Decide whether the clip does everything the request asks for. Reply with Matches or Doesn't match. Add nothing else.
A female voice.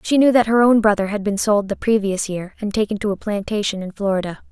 Matches